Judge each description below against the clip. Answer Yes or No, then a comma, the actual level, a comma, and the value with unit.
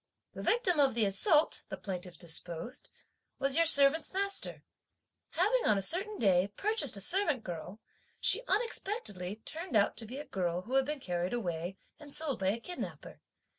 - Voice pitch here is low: No, very high, 255 Hz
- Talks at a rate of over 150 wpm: Yes, average, 170 wpm